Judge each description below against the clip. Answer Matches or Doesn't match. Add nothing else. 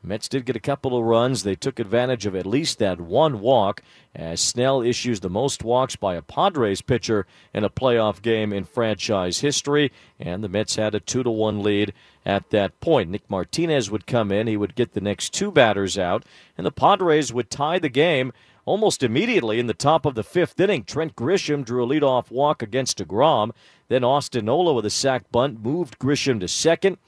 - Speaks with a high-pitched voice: Doesn't match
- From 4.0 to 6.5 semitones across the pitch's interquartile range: Matches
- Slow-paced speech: Doesn't match